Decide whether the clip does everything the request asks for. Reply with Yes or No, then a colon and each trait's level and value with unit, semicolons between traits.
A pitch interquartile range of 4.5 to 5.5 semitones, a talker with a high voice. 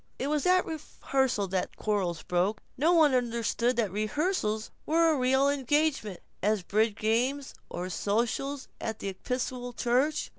Yes: average, 5.1 semitones; high, 245 Hz